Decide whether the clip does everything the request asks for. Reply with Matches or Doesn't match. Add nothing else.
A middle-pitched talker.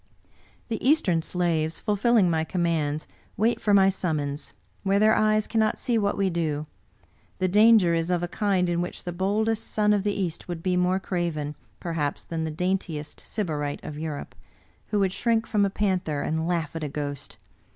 Matches